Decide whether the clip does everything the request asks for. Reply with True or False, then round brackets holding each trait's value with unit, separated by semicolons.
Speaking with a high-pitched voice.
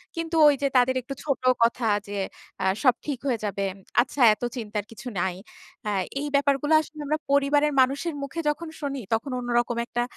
True (270 Hz)